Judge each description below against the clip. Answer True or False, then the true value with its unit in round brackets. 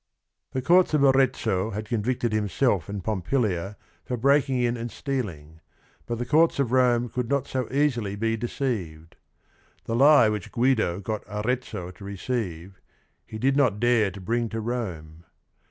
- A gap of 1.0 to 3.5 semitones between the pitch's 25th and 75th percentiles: False (4.2 semitones)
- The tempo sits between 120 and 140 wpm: False (160 wpm)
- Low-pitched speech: True (115 Hz)